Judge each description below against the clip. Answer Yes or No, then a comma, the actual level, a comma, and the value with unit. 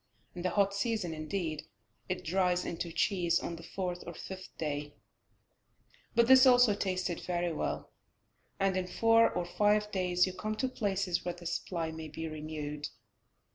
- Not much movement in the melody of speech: No, average, 3.3 semitones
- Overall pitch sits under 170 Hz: No, medium, 180 Hz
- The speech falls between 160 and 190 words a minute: Yes, average, 165 wpm